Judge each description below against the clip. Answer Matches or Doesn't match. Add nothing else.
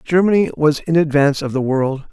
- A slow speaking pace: Doesn't match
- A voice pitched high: Doesn't match